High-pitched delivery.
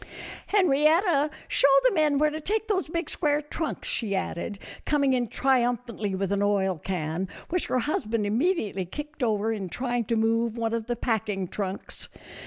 Yes: high, 235 Hz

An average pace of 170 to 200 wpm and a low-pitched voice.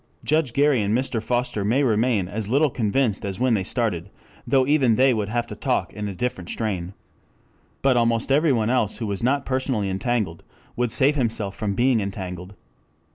Yes: average, 185 wpm; low, 115 Hz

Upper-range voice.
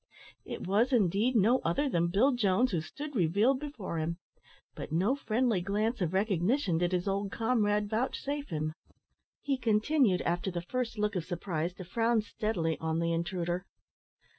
Yes: high, 200 Hz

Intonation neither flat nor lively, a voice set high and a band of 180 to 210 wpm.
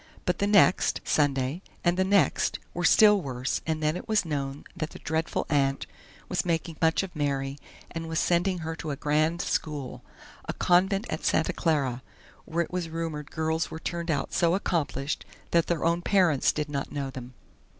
No: average, 3.3 semitones; medium, 160 Hz; average, 185 wpm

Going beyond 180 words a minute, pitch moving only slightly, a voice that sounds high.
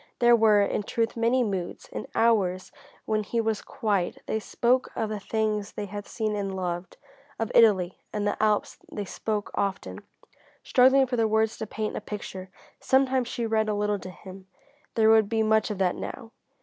Yes: average, 190 wpm; narrow, 2.0 semitones; high, 215 Hz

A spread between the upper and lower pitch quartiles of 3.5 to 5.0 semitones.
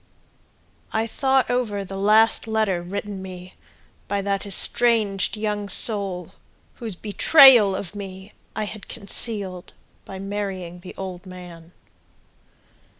No: narrow, 2.6 semitones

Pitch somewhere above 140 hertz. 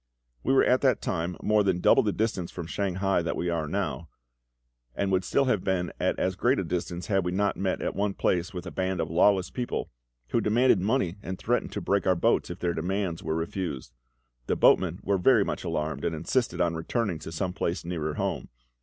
No: very low, 90 Hz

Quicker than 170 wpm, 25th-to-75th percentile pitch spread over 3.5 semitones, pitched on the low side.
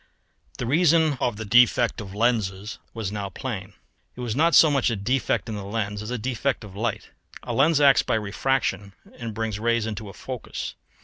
Yes: average, 195 wpm; average, 3.9 semitones; low, 115 Hz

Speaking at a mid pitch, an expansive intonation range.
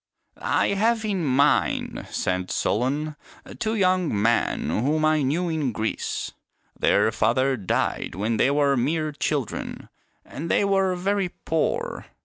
Yes: medium, 150 Hz; wide, 6.8 semitones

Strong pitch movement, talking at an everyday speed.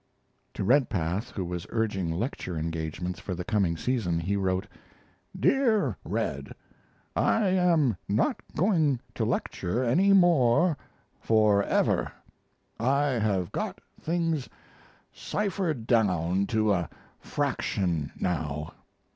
No: wide, 8.4 semitones; slow, 105 wpm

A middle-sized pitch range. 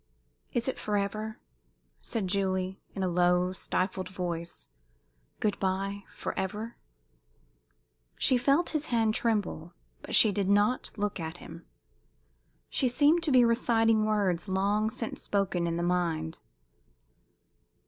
Yes: average, 3.7 semitones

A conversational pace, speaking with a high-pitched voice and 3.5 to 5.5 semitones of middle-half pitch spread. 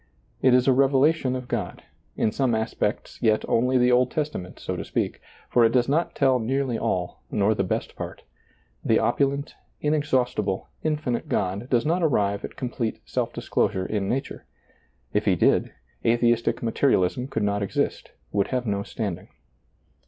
No: average, 165 wpm; low, 125 Hz; average, 4.0 semitones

